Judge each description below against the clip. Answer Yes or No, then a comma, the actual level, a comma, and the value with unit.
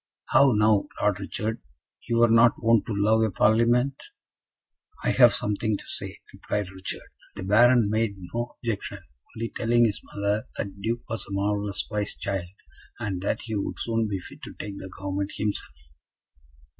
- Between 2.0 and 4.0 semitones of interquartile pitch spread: Yes, narrow, 2.5 semitones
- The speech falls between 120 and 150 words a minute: No, average, 170 wpm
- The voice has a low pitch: Yes, low, 105 Hz